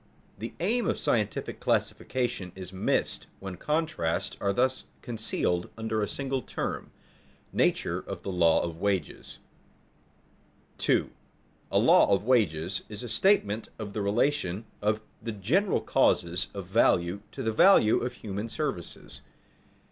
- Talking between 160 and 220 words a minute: No, average, 140 wpm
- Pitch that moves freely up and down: No, average, 4.4 semitones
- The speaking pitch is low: Yes, low, 105 Hz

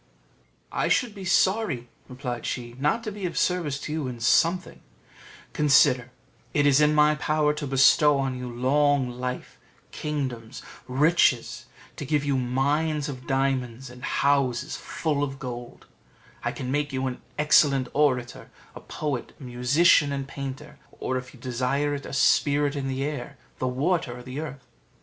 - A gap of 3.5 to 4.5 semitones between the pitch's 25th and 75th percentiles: No, average, 2.8 semitones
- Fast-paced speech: No, average, 160 wpm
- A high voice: No, medium, 140 Hz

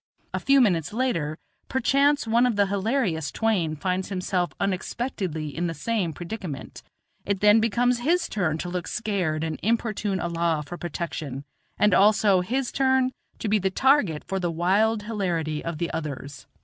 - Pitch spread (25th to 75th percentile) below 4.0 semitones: No, average, 5.3 semitones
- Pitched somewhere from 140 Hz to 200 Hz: Yes, high, 190 Hz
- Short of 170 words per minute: Yes, average, 160 wpm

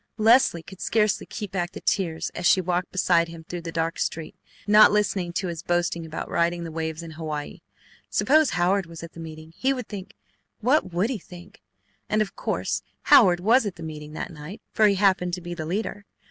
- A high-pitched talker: No, medium, 175 Hz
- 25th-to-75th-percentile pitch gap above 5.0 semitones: No, average, 3.7 semitones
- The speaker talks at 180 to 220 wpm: Yes, fast, 205 wpm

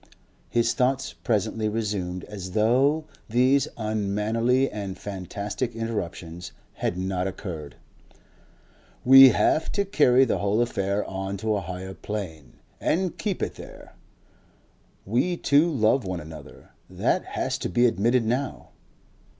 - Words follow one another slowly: Yes, slow, 125 wpm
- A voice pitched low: Yes, low, 110 Hz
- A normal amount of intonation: Yes, average, 4.9 semitones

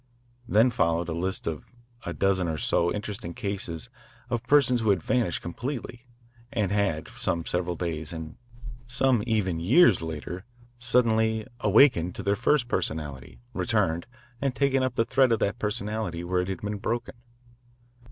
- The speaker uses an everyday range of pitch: No, wide, 5.8 semitones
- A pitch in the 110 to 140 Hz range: No, low, 100 Hz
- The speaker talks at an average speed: Yes, average, 155 wpm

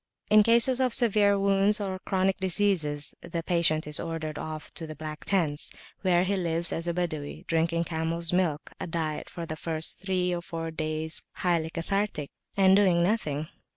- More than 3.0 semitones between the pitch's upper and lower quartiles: Yes, average, 3.4 semitones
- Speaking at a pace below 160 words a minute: No, average, 175 wpm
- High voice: No, medium, 170 Hz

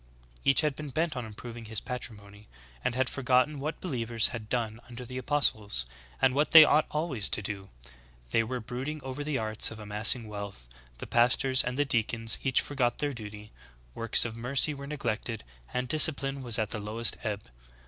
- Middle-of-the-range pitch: No, low, 120 Hz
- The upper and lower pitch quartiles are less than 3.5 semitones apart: No, average, 4.1 semitones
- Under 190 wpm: No, average, 195 wpm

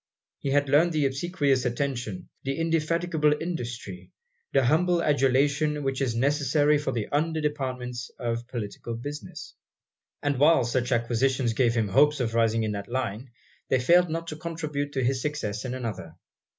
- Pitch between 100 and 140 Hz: Yes, low, 135 Hz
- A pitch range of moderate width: Yes, average, 3.9 semitones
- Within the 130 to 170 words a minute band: Yes, average, 160 wpm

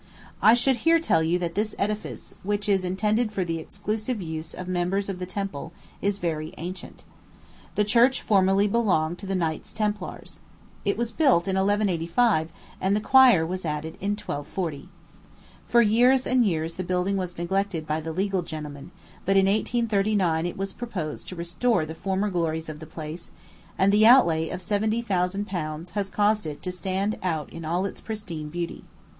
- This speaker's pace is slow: No, average, 180 wpm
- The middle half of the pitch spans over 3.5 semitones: Yes, average, 4.0 semitones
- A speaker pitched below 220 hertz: Yes, high, 190 Hz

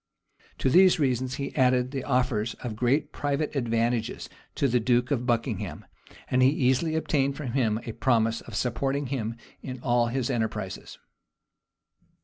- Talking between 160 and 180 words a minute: No, average, 150 wpm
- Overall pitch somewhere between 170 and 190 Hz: No, low, 125 Hz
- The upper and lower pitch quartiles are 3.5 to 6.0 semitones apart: No, average, 2.7 semitones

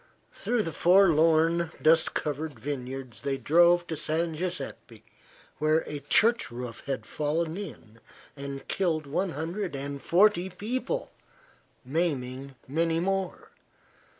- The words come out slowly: Yes, slow, 120 wpm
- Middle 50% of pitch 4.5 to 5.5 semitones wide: No, average, 4.0 semitones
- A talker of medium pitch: Yes, medium, 160 Hz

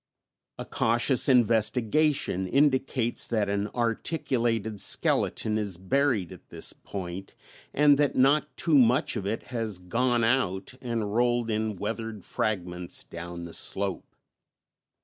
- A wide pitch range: No, average, 4.0 semitones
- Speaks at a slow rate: Yes, slow, 125 wpm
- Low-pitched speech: Yes, low, 115 Hz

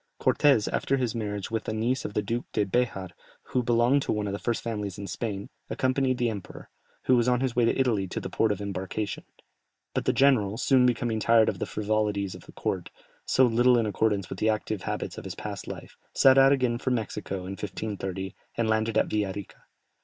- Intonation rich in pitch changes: No, average, 3.3 semitones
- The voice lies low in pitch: Yes, low, 110 Hz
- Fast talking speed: Yes, fast, 220 wpm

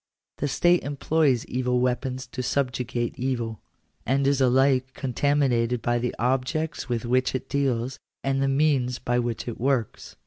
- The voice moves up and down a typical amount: No, narrow, 2.0 semitones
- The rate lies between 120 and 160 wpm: Yes, average, 150 wpm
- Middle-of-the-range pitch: No, low, 130 Hz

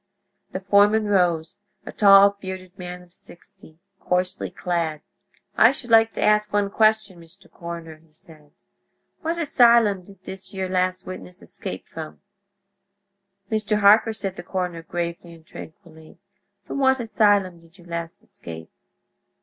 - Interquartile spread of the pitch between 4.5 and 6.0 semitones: No, average, 3.4 semitones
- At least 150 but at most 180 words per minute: No, average, 140 wpm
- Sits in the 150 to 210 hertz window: Yes, medium, 185 Hz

